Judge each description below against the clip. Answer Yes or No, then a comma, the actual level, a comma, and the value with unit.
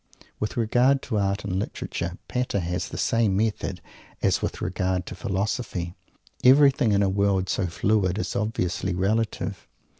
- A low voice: Yes, low, 100 Hz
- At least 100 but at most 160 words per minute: Yes, average, 150 wpm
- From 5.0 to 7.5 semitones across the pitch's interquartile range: No, average, 3.4 semitones